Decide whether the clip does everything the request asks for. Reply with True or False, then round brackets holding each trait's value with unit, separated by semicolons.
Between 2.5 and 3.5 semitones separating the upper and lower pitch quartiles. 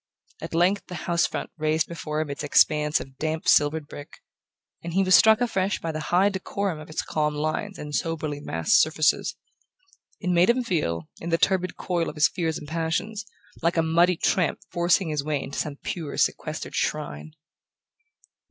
True (3.1 semitones)